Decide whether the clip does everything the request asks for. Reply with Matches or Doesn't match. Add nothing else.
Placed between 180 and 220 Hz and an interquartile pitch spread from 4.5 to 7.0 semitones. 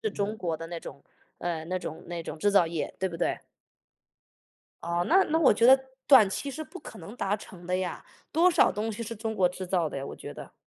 Matches